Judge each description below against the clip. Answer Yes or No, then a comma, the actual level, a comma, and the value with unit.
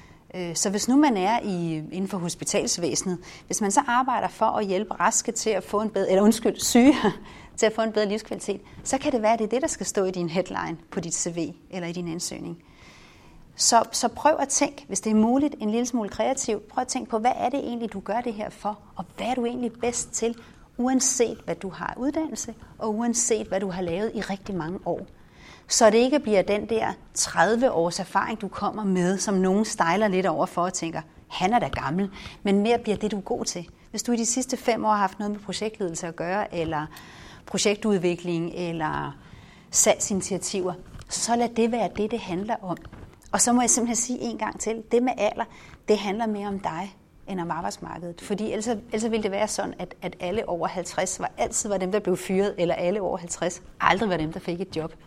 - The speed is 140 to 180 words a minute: No, fast, 225 wpm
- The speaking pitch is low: No, high, 205 Hz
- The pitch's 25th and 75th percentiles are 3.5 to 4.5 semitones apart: Yes, average, 4.2 semitones